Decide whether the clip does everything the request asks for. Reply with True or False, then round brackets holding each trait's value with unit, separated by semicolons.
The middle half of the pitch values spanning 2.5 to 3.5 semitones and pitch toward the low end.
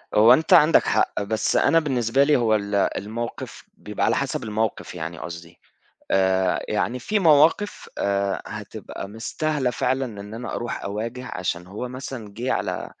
False (4.6 semitones; 115 Hz)